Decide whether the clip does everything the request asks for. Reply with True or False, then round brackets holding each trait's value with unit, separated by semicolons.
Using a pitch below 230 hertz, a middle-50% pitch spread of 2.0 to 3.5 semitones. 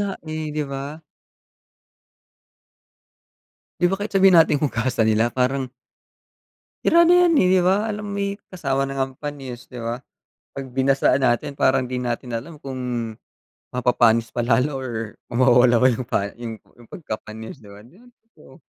False (135 Hz; 4.5 semitones)